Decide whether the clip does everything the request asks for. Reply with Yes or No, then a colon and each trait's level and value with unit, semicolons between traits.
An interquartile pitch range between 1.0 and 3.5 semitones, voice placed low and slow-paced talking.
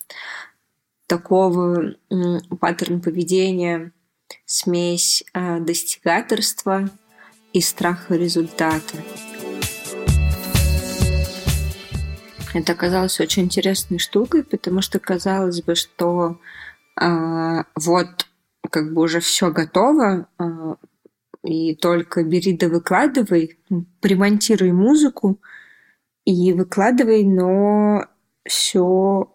No: narrow, 2.4 semitones; medium, 175 Hz; slow, 75 wpm